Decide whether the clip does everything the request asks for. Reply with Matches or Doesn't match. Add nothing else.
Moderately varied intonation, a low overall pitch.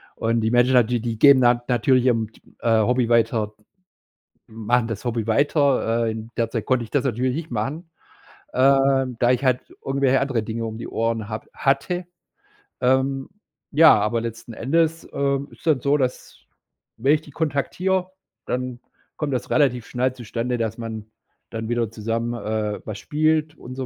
Matches